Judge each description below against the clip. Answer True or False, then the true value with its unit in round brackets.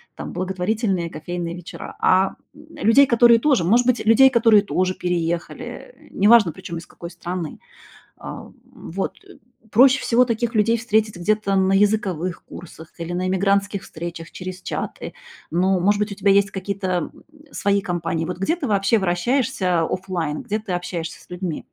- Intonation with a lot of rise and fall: False (3.7 semitones)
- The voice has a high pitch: True (195 Hz)